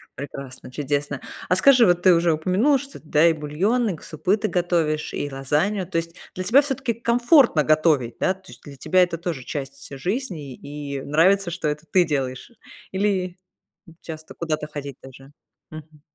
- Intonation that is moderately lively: Yes, average, 4.5 semitones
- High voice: No, medium, 165 Hz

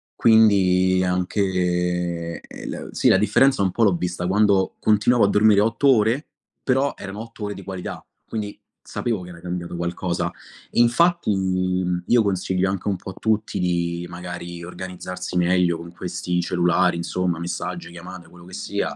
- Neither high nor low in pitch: No, very low, 90 Hz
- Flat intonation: No, average, 3.0 semitones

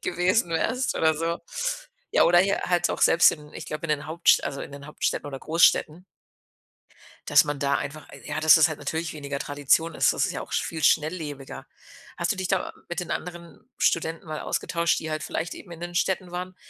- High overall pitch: No, medium, 160 Hz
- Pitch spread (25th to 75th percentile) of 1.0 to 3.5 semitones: Yes, narrow, 2.6 semitones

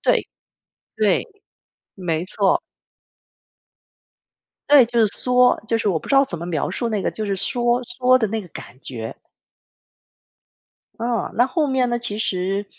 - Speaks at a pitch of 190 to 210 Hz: No, high, 220 Hz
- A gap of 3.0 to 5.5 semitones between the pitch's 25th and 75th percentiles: Yes, average, 4.7 semitones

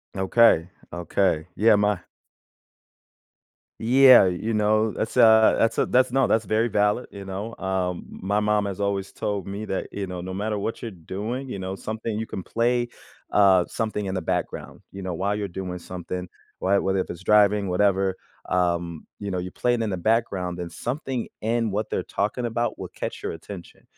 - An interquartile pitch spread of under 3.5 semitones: Yes, average, 3.1 semitones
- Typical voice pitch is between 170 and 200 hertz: No, low, 100 Hz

